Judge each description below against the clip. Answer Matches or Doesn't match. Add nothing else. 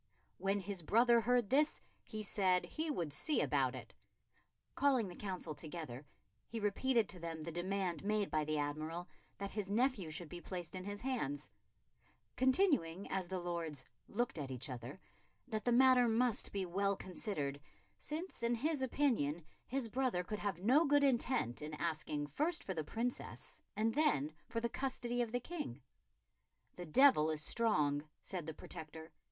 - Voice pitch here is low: Doesn't match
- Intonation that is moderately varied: Doesn't match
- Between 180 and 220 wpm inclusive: Doesn't match